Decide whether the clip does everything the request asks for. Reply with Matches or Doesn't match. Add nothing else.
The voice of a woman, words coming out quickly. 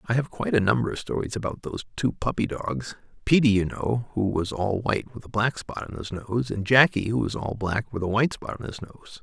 Doesn't match